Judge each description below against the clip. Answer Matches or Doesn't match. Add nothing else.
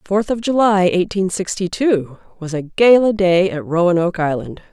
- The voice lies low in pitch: Doesn't match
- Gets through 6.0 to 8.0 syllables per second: Doesn't match